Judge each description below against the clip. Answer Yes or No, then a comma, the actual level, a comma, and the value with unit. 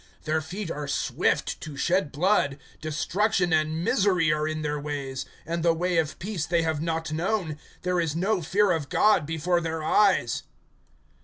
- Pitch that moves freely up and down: No, average, 2.9 semitones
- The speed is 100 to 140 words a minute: No, average, 170 wpm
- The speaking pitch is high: No, medium, 165 Hz